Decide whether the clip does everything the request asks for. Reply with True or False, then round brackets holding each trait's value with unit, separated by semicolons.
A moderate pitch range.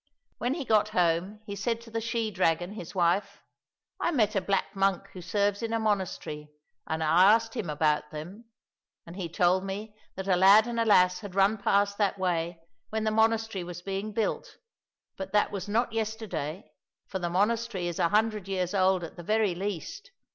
True (3.5 semitones)